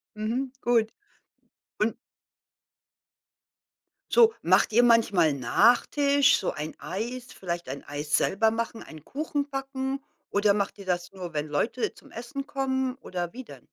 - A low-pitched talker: No, high, 230 Hz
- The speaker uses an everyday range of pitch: No, wide, 6.9 semitones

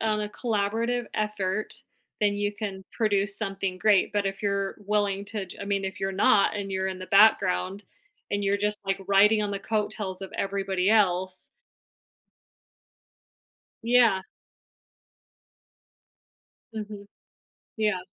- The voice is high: Yes, high, 200 Hz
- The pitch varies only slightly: Yes, narrow, 1.5 semitones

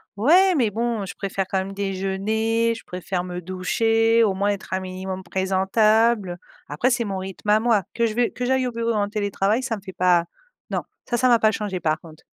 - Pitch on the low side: No, high, 205 Hz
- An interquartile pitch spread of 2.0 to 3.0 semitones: No, average, 3.4 semitones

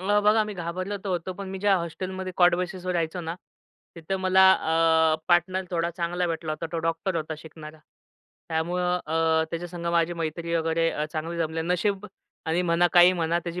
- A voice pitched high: No, medium, 170 Hz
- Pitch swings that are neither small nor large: No, narrow, 2.1 semitones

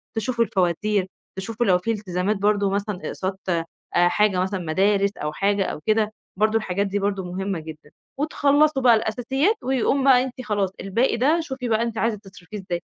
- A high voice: Yes, high, 205 Hz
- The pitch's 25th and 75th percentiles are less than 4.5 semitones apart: Yes, average, 3.6 semitones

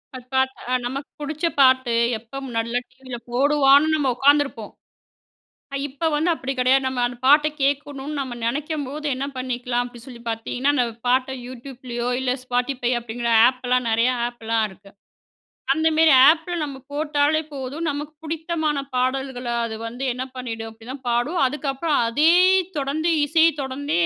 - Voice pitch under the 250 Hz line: No, very high, 265 Hz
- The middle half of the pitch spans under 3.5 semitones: Yes, average, 3.1 semitones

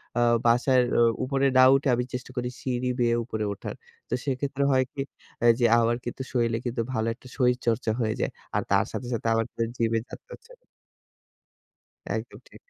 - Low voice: Yes, low, 125 Hz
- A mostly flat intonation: Yes, narrow, 1.9 semitones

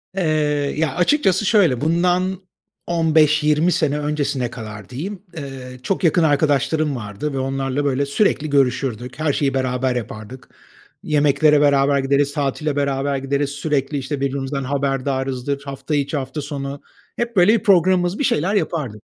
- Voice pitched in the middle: Yes, medium, 145 Hz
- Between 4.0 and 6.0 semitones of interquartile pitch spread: No, narrow, 2.6 semitones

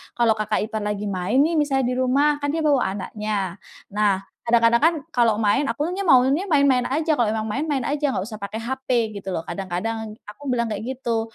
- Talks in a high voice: Yes, high, 235 Hz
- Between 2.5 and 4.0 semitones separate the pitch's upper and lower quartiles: No, average, 4.5 semitones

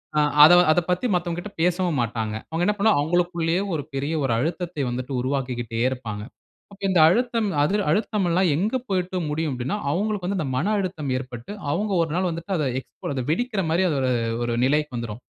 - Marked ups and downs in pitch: Yes, wide, 5.8 semitones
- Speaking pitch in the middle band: Yes, medium, 165 Hz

